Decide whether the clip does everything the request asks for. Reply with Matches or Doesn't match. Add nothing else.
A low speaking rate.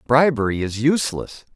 Matches